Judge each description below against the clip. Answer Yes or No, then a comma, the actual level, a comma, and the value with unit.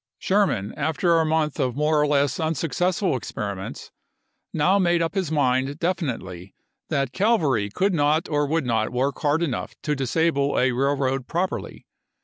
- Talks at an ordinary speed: Yes, average, 160 wpm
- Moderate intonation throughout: Yes, average, 4.2 semitones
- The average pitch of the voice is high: No, medium, 145 Hz